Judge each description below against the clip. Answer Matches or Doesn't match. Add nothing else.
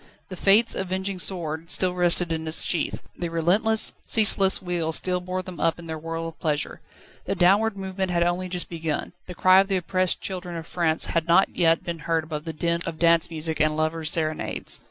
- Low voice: Doesn't match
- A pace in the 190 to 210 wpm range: Matches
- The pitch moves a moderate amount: Doesn't match